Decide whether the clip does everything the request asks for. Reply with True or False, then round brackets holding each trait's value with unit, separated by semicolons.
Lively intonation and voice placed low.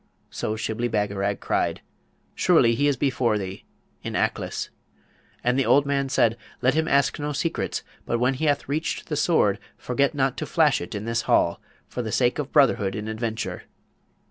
False (4.4 semitones; 125 Hz)